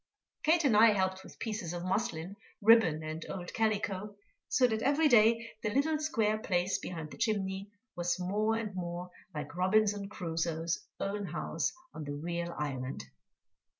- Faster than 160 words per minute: No, average, 155 wpm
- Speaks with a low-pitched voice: No, high, 195 Hz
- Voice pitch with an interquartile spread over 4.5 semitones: No, average, 4.1 semitones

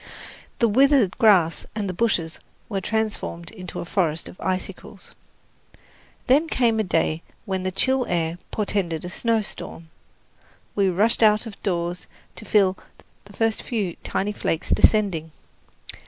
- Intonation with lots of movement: No, average, 4.2 semitones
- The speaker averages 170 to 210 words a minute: No, average, 140 wpm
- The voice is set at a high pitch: Yes, high, 195 Hz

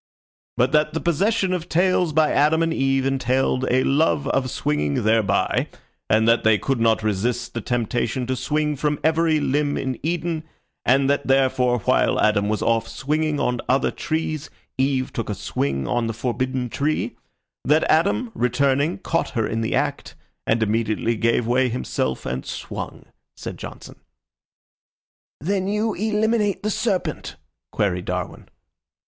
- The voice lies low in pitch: Yes, low, 130 Hz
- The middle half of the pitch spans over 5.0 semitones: Yes, wide, 5.4 semitones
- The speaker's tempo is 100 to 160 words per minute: Yes, average, 155 wpm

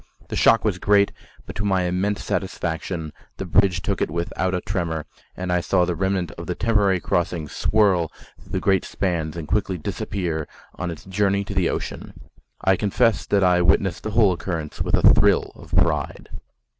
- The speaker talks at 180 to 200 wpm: Yes, average, 185 wpm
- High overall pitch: No, very low, 90 Hz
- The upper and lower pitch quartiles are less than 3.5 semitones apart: Yes, narrow, 2.6 semitones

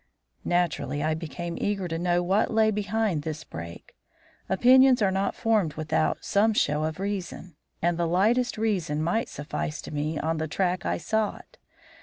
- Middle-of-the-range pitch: Yes, medium, 175 Hz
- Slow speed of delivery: No, average, 170 wpm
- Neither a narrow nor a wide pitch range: Yes, average, 4.9 semitones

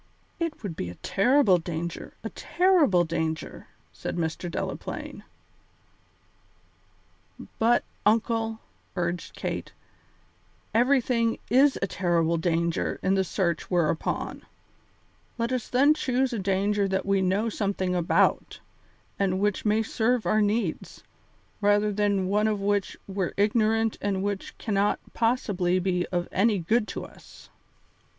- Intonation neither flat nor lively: Yes, average, 3.9 semitones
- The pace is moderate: No, slow, 130 wpm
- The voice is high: Yes, high, 200 Hz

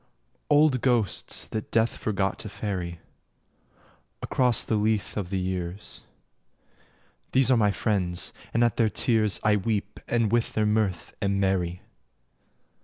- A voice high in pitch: No, low, 105 Hz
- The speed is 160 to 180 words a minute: No, slow, 135 wpm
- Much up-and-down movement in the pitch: No, average, 3.1 semitones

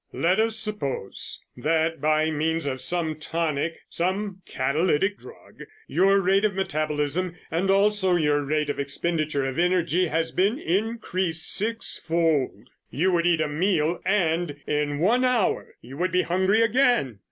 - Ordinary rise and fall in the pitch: Yes, average, 4.2 semitones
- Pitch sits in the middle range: Yes, medium, 170 Hz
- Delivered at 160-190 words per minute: No, average, 150 wpm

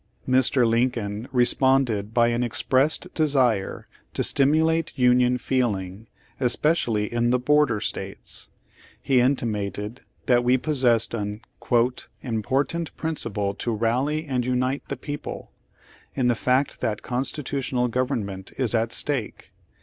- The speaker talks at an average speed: No, slow, 120 wpm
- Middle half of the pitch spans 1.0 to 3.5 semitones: Yes, average, 3.1 semitones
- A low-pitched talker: Yes, low, 125 Hz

